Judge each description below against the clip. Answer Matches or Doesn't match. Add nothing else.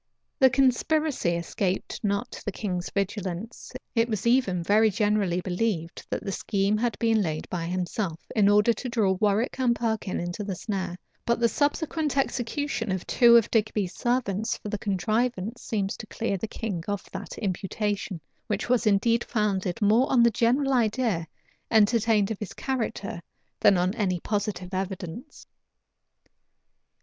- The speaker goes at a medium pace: Matches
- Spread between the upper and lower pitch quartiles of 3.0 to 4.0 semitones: Matches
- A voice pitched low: Doesn't match